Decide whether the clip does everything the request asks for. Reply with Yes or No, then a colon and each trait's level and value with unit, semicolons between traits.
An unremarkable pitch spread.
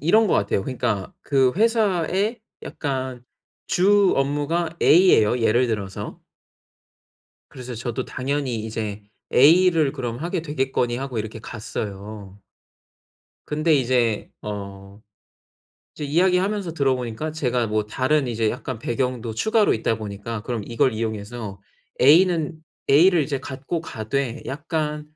No: wide, 5.9 semitones